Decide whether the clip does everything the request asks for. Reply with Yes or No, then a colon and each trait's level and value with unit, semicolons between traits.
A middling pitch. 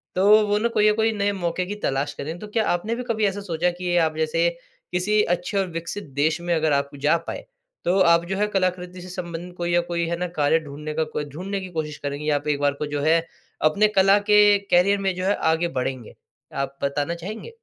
Yes: medium, 175 Hz